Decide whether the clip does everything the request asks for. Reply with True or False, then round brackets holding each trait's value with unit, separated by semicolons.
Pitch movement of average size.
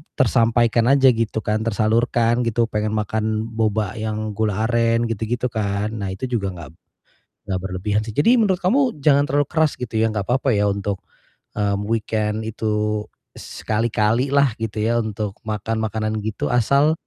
False (1.9 semitones)